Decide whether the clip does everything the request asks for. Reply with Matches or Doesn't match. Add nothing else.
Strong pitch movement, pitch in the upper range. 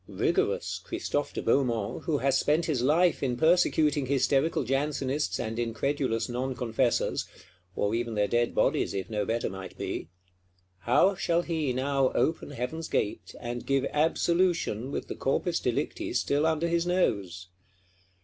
Doesn't match